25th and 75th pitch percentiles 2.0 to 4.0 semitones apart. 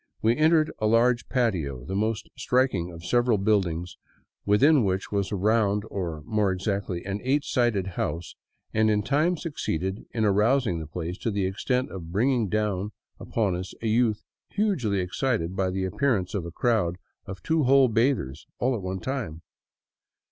No: average, 4.8 semitones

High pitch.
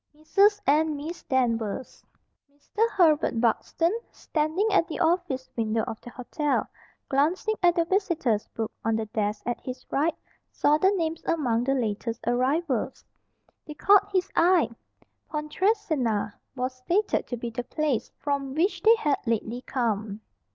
Yes: very high, 285 Hz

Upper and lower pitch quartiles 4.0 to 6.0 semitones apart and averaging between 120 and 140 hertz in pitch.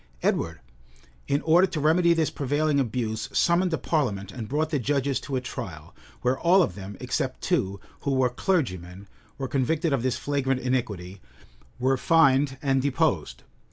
Yes: average, 4.4 semitones; low, 135 Hz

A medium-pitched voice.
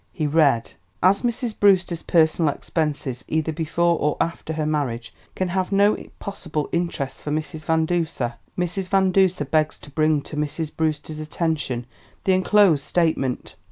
Yes: medium, 160 Hz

